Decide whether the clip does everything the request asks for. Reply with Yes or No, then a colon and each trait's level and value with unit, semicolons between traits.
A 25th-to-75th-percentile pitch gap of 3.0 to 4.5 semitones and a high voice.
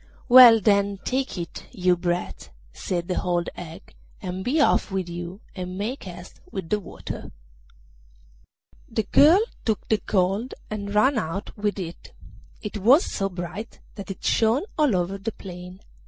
Yes: average, 3.7 semitones; high, 195 Hz